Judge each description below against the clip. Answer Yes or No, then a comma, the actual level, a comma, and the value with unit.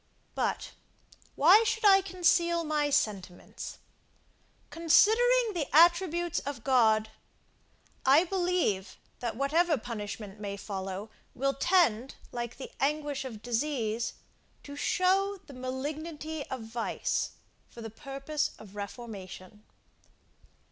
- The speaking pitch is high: Yes, very high, 275 Hz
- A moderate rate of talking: No, slow, 105 wpm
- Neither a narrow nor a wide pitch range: No, wide, 7.3 semitones